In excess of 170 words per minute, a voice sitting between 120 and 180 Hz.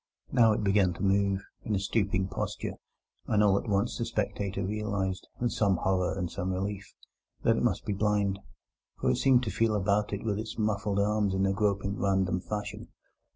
No: average, 200 wpm; low, 100 Hz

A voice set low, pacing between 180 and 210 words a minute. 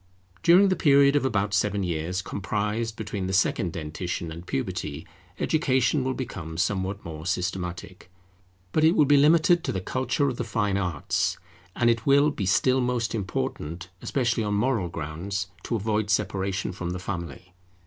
No: low, 100 Hz; average, 165 wpm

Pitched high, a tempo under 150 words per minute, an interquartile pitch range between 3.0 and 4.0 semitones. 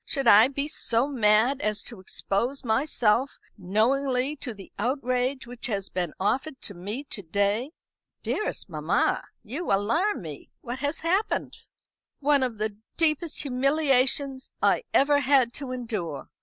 No: very high, 255 Hz; average, 140 wpm; average, 4.8 semitones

